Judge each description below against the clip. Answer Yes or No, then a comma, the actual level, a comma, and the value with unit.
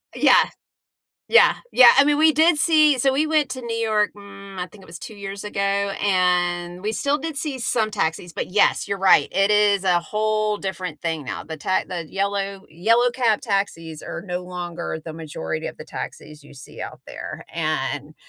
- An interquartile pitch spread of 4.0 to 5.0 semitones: Yes, average, 4.5 semitones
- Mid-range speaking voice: No, high, 200 Hz